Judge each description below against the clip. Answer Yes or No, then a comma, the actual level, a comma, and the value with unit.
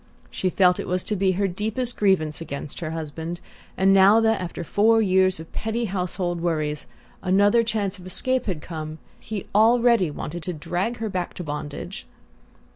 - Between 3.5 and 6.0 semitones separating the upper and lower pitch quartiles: Yes, average, 4.0 semitones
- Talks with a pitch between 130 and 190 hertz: Yes, medium, 185 Hz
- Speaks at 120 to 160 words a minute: No, average, 175 wpm